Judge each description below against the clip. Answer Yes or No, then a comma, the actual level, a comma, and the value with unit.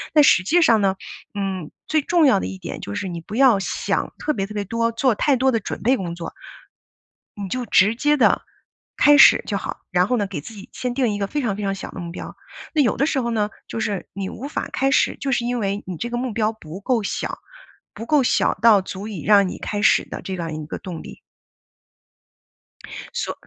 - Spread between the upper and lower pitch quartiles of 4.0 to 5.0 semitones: Yes, average, 4.7 semitones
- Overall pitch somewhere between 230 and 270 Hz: No, high, 215 Hz